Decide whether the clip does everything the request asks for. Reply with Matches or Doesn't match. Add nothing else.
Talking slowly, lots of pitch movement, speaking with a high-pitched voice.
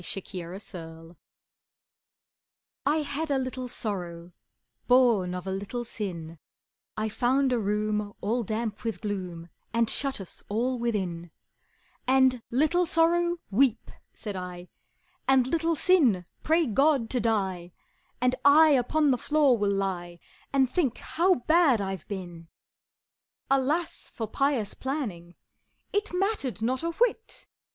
Matches